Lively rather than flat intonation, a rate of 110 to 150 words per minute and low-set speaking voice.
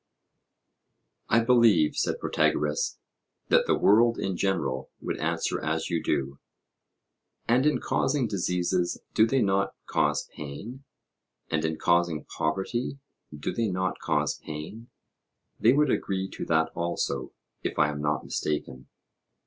Yes: wide, 7.0 semitones; slow, 135 wpm; very low, 90 Hz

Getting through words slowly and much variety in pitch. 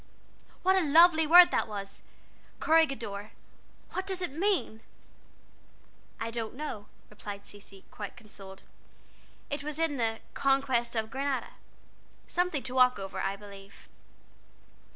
Yes: slow, 125 wpm; wide, 7.3 semitones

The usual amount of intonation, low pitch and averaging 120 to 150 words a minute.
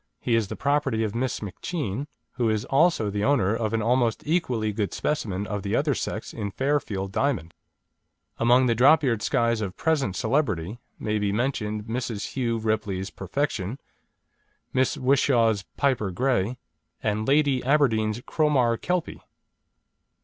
Yes: average, 4.5 semitones; low, 115 Hz; average, 145 wpm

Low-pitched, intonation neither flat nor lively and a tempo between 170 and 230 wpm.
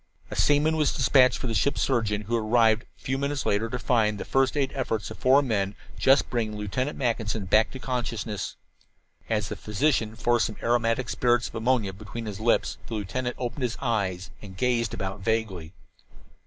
Yes: low, 115 Hz; average, 3.2 semitones; average, 190 wpm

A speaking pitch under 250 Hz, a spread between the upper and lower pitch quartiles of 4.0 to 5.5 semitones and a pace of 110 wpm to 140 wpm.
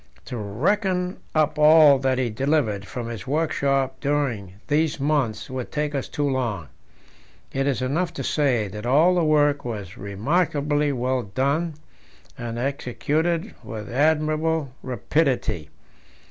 Yes: medium, 140 Hz; average, 4.4 semitones; slow, 135 wpm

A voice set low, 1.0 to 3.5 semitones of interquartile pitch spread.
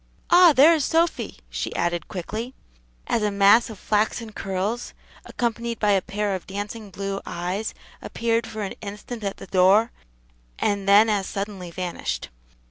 No: high, 205 Hz; average, 2.8 semitones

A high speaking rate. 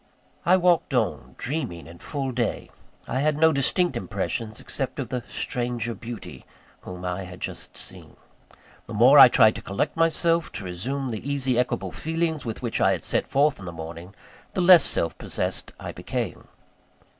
No: average, 175 wpm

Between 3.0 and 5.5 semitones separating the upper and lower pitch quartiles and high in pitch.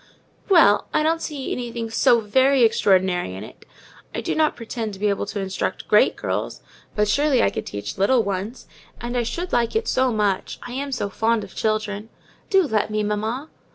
Yes: average, 4.2 semitones; high, 225 Hz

